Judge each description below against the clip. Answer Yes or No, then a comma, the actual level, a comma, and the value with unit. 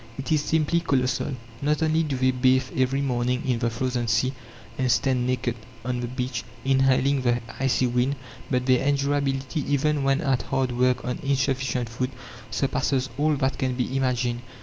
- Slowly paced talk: No, average, 170 wpm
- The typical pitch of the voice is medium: No, low, 130 Hz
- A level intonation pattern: Yes, narrow, 1.6 semitones